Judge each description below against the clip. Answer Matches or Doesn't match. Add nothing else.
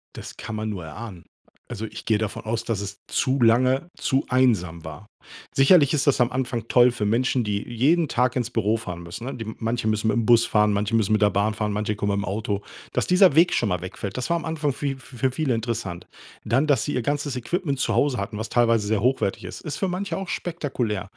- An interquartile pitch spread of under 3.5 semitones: Doesn't match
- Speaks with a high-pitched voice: Doesn't match